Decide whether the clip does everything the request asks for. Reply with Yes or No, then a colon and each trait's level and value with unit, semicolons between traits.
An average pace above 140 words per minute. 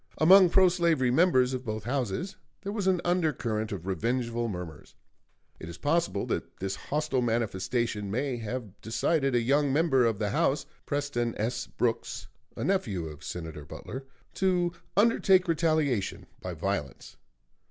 Yes: average, 150 wpm